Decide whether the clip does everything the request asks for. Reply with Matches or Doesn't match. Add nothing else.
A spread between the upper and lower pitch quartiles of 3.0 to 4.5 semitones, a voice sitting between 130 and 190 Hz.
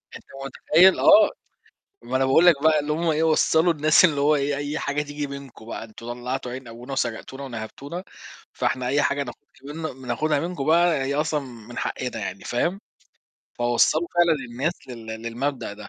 Matches